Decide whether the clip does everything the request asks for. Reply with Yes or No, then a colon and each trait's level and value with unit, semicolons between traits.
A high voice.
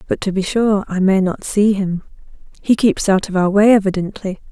Yes: high, 195 Hz